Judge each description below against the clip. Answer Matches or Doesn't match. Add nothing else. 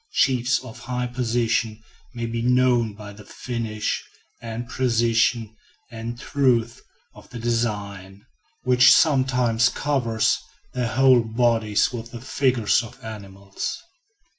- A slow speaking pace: Matches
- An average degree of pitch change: Doesn't match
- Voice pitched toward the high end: Doesn't match